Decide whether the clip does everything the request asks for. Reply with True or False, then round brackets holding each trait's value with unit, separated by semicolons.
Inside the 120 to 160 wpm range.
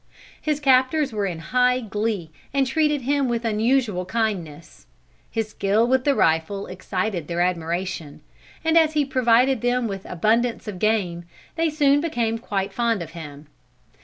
True (155 wpm)